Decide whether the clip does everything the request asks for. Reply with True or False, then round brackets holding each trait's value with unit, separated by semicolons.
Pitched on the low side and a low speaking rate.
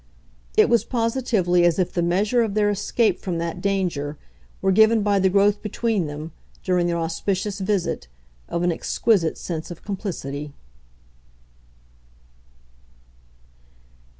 False (190 Hz; 125 wpm)